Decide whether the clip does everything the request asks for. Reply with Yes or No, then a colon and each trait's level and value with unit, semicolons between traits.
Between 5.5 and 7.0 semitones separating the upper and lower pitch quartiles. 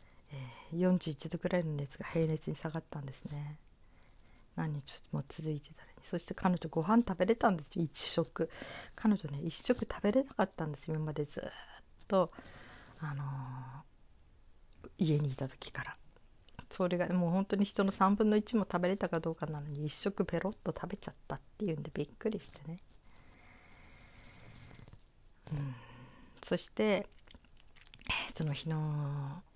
No: average, 5.1 semitones